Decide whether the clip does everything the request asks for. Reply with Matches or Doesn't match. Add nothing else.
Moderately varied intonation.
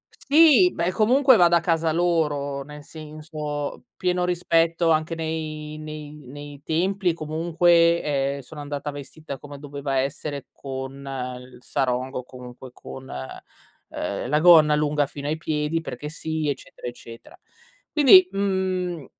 Matches